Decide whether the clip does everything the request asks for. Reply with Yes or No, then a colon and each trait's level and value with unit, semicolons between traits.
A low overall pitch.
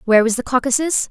No: very high, 255 Hz